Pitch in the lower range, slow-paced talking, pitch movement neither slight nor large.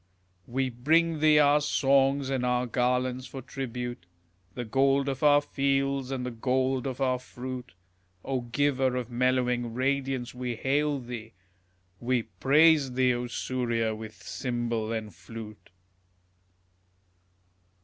No: low, 125 Hz; slow, 130 wpm; narrow, 2.1 semitones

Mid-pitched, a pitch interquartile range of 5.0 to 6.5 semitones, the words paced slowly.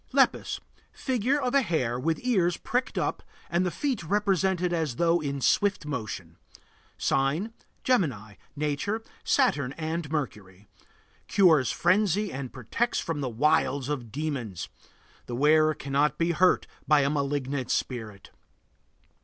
Yes: medium, 155 Hz; wide, 5.6 semitones; slow, 130 wpm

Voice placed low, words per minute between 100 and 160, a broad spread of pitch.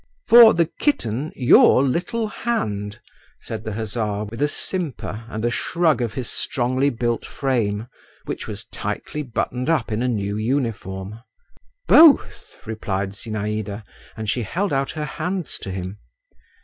Yes: low, 120 Hz; average, 140 wpm; wide, 5.7 semitones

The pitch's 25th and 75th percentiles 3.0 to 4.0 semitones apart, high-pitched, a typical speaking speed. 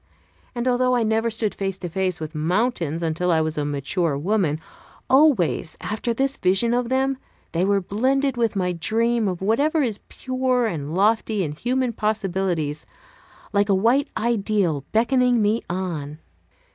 No: wide, 5.6 semitones; high, 205 Hz; average, 160 wpm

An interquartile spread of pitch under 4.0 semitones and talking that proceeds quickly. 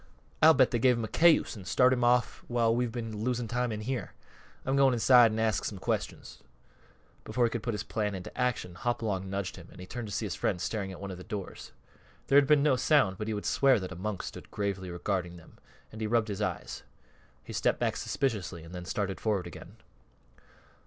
No: average, 4.3 semitones; fast, 225 wpm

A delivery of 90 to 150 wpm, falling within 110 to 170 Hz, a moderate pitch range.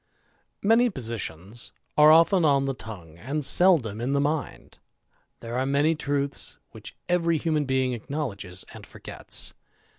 Yes: average, 140 wpm; medium, 140 Hz; average, 5.0 semitones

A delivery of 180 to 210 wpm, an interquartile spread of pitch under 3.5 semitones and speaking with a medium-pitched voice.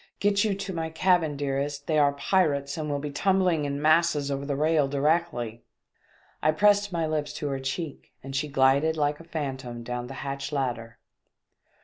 Yes: average, 185 wpm; average, 3.0 semitones; medium, 145 Hz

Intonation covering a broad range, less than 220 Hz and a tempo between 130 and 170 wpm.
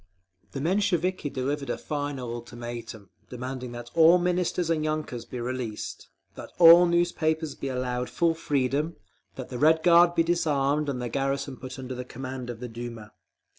No: average, 4.7 semitones; low, 135 Hz; average, 165 wpm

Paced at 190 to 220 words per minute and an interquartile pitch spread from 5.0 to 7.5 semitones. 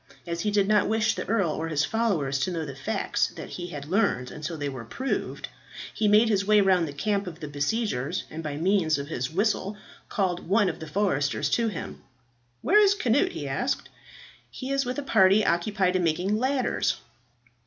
Yes: average, 200 wpm; wide, 5.6 semitones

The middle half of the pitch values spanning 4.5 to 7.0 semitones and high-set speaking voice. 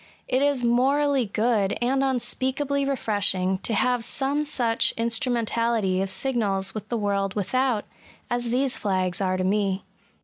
Yes: average, 4.8 semitones; high, 235 Hz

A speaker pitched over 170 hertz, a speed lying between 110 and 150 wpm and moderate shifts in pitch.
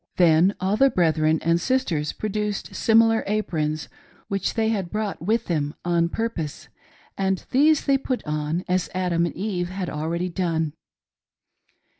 Yes: medium, 185 Hz; average, 145 wpm; average, 4.6 semitones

